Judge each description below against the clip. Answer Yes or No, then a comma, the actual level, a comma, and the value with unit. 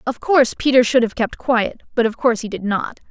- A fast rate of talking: Yes, fast, 250 wpm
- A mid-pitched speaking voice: No, high, 235 Hz